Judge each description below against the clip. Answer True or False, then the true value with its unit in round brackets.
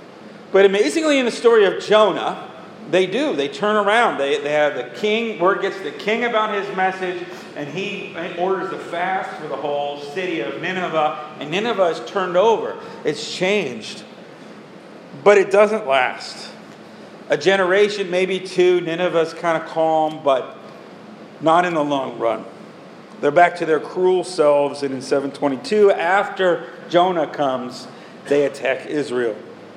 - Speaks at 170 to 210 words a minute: False (155 wpm)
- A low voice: False (180 Hz)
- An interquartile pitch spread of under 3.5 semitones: False (4.5 semitones)